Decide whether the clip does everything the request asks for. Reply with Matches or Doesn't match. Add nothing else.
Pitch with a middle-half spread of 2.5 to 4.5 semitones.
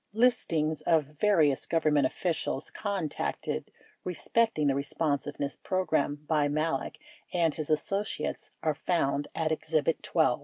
Matches